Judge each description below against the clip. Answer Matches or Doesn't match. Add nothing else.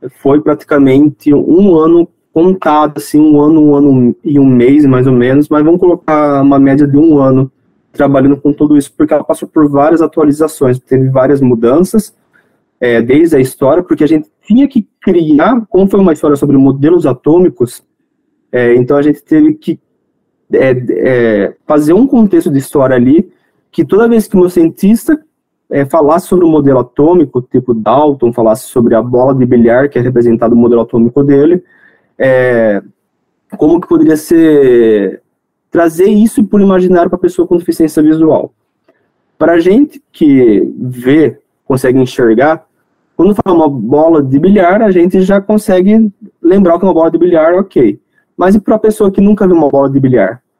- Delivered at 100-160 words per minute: Doesn't match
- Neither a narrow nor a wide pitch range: Doesn't match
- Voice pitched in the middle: Matches